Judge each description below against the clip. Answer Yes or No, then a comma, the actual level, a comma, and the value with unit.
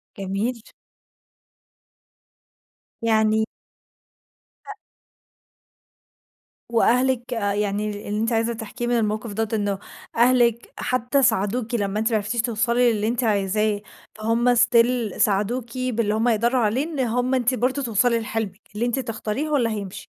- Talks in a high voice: Yes, high, 230 Hz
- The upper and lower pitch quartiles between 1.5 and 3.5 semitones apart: Yes, narrow, 2.5 semitones